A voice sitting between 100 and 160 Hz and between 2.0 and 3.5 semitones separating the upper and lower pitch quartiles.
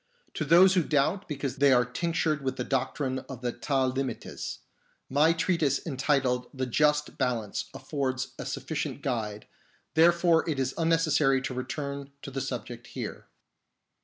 Yes: low, 135 Hz; average, 3.0 semitones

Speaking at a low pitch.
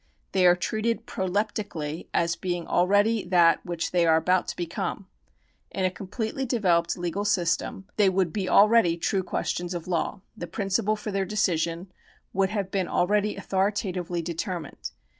No: medium, 185 Hz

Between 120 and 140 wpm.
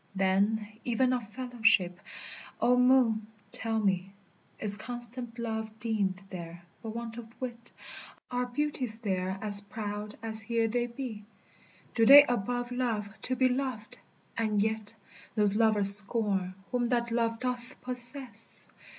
Yes: slow, 135 wpm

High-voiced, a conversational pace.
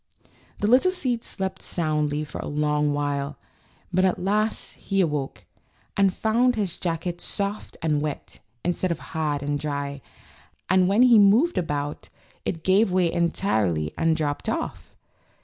No: medium, 170 Hz; average, 150 wpm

